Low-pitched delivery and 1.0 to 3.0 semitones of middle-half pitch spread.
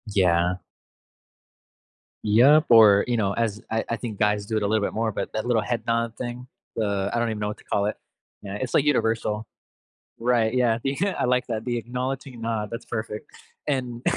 Yes: low, 115 Hz; narrow, 2.5 semitones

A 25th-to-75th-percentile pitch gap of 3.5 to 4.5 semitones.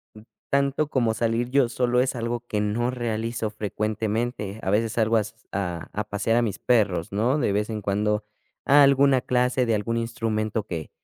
No: narrow, 2.5 semitones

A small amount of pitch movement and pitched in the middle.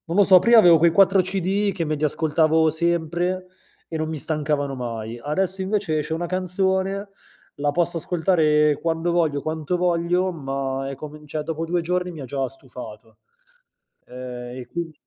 No: average, 3.6 semitones; medium, 160 Hz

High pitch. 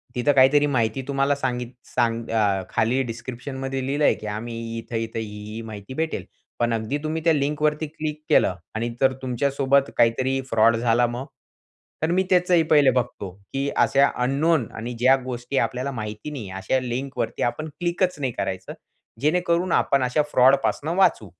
No: low, 130 Hz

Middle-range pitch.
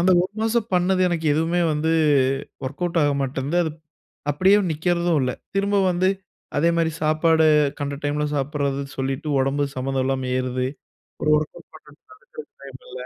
Yes: medium, 155 Hz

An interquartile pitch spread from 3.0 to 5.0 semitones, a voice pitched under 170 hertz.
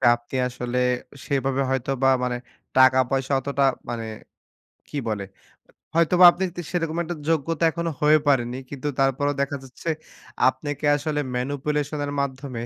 No: narrow, 2.6 semitones; medium, 140 Hz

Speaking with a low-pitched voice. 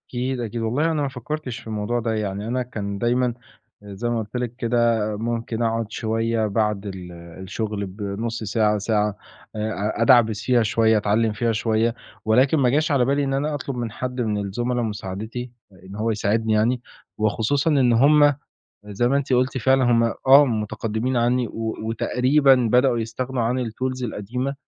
Yes: low, 115 Hz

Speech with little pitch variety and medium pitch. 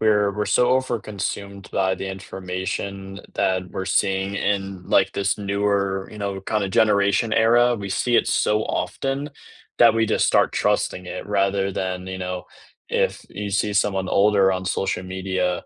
No: narrow, 1.6 semitones; low, 100 Hz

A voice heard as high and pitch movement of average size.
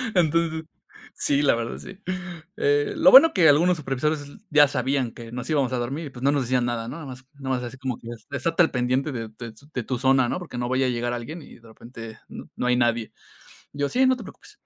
No: low, 130 Hz; average, 3.9 semitones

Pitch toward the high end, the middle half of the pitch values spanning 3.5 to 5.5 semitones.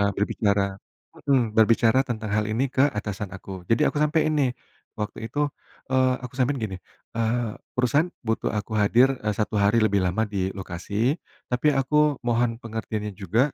No: low, 115 Hz; average, 3.8 semitones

